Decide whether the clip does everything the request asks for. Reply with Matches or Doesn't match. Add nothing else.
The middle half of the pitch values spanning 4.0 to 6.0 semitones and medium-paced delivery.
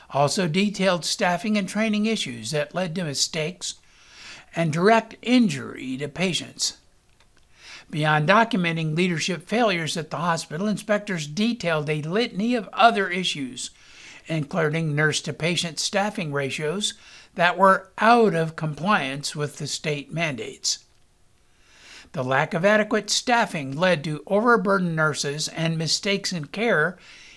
Doesn't match